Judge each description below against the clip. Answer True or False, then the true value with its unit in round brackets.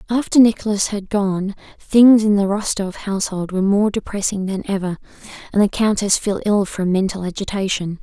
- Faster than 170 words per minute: False (165 wpm)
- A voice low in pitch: False (200 Hz)